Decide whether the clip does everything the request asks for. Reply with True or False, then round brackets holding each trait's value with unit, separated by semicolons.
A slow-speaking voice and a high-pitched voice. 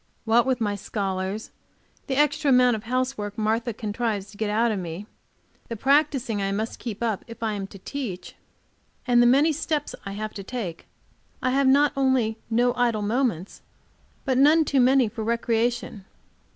False (175 wpm; 230 Hz)